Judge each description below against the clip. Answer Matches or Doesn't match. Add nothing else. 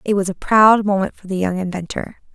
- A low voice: Doesn't match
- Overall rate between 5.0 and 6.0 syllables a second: Matches